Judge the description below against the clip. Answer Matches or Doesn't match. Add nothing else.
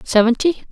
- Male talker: Doesn't match